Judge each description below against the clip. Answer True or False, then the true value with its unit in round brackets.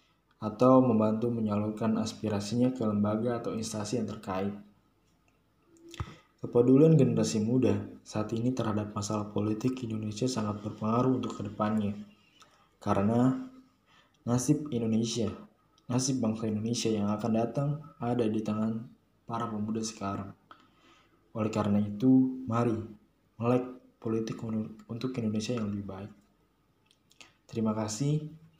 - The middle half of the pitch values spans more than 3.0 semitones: False (2.6 semitones)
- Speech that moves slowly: False (105 wpm)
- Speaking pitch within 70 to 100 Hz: False (110 Hz)